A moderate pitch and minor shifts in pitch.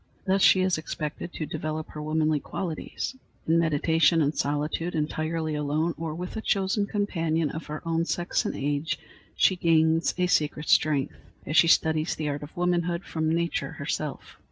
Yes: medium, 160 Hz; narrow, 2.0 semitones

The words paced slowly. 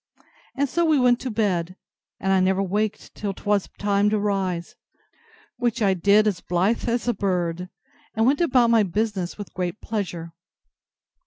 No: average, 165 wpm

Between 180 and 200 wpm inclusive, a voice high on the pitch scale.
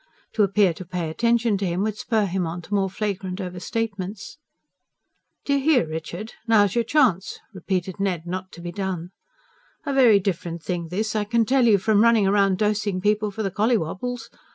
Yes: average, 185 wpm; high, 200 Hz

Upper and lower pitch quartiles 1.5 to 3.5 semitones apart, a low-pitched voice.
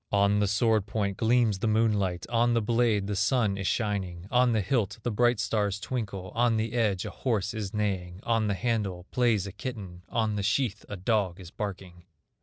Yes: average, 2.9 semitones; low, 105 Hz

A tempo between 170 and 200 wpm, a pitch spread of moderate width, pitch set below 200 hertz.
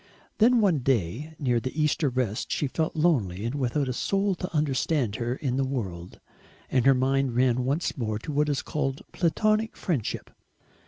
Yes: average, 175 wpm; average, 4.2 semitones; low, 135 Hz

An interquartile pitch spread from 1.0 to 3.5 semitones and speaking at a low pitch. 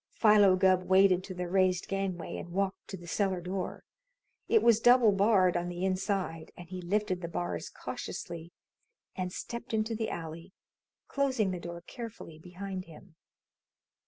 No: narrow, 2.6 semitones; medium, 185 Hz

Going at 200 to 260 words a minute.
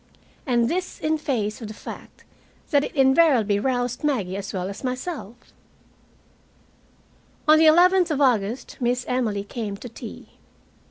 No: average, 145 wpm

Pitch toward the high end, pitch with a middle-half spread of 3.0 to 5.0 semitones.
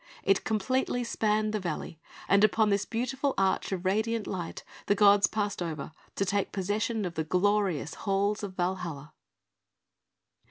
No: high, 200 Hz; narrow, 2.6 semitones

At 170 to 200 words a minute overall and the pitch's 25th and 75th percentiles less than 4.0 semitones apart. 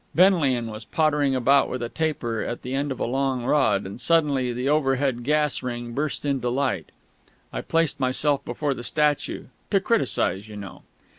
Yes: average, 175 wpm; average, 3.5 semitones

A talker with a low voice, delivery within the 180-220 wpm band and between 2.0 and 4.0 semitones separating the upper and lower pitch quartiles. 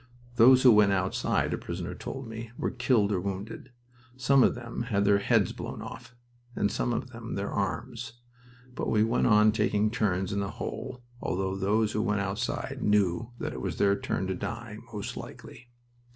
Yes: low, 110 Hz; average, 185 wpm; average, 3.0 semitones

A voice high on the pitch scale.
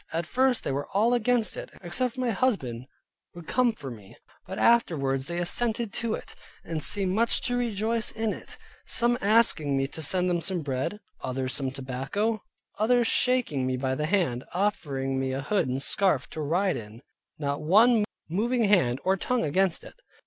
No: medium, 180 Hz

